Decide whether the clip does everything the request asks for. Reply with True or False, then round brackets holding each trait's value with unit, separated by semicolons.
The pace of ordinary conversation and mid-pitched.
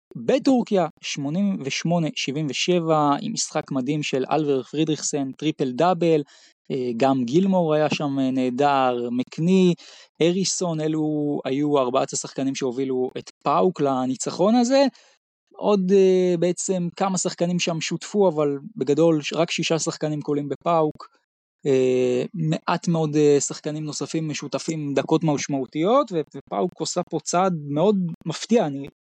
True (110 wpm; 155 Hz)